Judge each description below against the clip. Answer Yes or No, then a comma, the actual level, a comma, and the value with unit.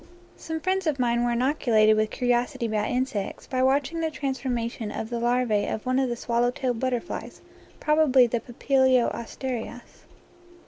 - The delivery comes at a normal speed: Yes, average, 165 wpm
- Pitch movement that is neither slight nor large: No, narrow, 2.2 semitones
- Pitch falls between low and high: No, high, 245 Hz